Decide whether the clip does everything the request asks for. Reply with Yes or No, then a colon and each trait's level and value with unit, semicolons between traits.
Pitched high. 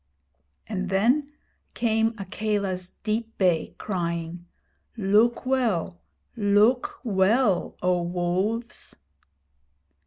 Yes: high, 205 Hz